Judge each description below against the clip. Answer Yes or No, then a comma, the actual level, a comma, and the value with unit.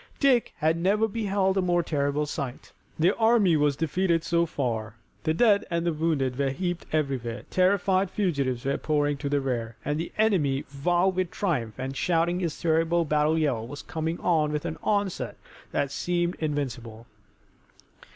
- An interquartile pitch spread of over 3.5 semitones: Yes, average, 4.4 semitones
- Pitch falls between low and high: Yes, medium, 160 Hz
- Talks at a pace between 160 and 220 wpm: Yes, average, 165 wpm